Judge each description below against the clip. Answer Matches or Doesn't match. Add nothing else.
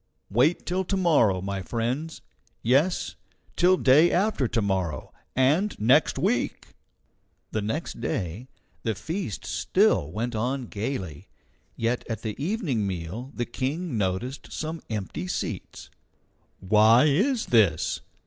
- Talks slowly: Matches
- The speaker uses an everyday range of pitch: Doesn't match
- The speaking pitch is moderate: Doesn't match